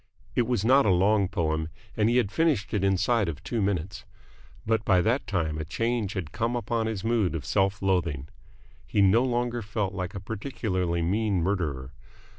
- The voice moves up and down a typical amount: Yes, average, 4.1 semitones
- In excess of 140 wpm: Yes, average, 185 wpm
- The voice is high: No, low, 100 Hz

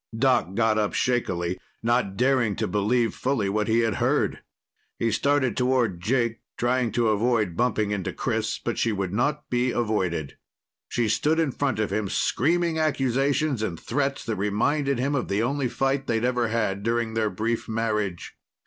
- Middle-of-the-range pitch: No, low, 115 Hz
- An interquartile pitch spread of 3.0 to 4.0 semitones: Yes, average, 3.7 semitones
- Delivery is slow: No, average, 170 wpm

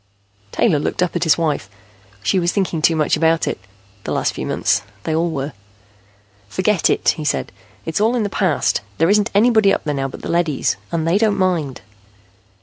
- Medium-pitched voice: Yes, medium, 170 Hz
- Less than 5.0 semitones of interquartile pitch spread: Yes, average, 4.2 semitones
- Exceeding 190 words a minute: Yes, average, 200 wpm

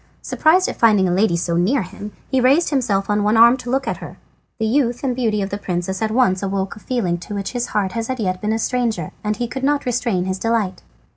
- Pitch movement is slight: No, average, 4.4 semitones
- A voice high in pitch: Yes, high, 220 Hz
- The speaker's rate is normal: No, fast, 255 wpm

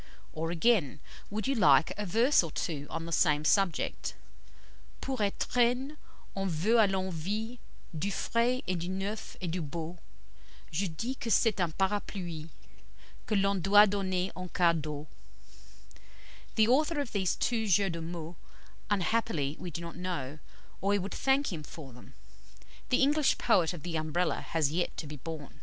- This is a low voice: No, medium, 185 Hz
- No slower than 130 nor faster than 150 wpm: No, average, 165 wpm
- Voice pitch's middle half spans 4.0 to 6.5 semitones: Yes, average, 5.0 semitones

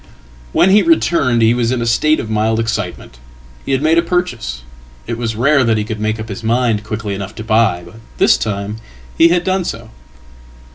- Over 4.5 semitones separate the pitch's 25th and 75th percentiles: No, average, 4.1 semitones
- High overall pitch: No, low, 115 Hz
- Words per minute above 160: Yes, average, 195 wpm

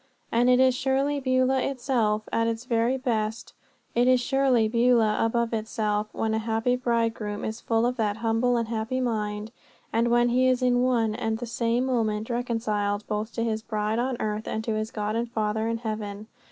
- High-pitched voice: Yes, high, 230 Hz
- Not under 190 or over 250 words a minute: Yes, average, 195 wpm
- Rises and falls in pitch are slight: Yes, narrow, 2.2 semitones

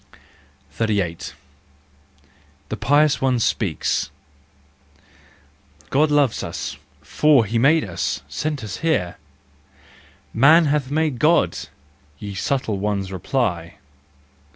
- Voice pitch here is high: No, low, 120 Hz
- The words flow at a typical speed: No, slow, 105 wpm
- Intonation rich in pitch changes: Yes, wide, 7.3 semitones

